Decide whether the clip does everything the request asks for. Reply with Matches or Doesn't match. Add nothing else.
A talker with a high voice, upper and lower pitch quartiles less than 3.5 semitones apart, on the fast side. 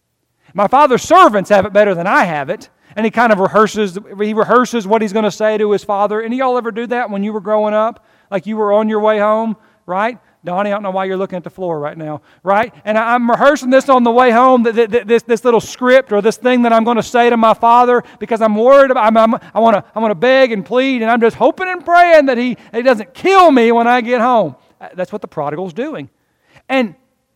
Matches